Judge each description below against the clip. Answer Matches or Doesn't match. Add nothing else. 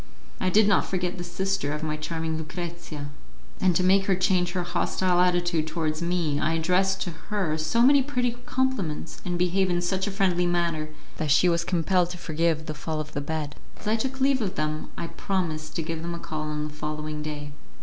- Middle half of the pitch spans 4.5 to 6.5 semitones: Doesn't match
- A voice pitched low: Doesn't match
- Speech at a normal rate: Doesn't match